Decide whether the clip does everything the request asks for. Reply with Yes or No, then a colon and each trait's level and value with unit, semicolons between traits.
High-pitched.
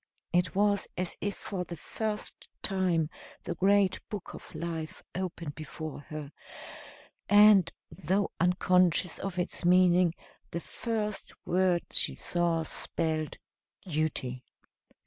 No: medium, 180 Hz